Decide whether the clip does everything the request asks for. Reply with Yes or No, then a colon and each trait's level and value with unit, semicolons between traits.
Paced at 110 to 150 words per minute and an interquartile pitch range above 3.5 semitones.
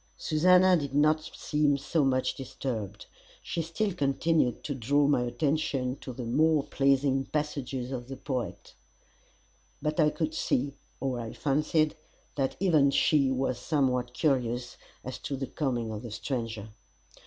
No: average, 145 wpm; average, 3.2 semitones